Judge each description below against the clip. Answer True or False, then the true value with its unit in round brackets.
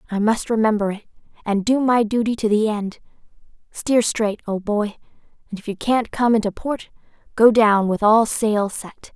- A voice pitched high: True (215 Hz)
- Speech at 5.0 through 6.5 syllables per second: False (4.7 syllables/s)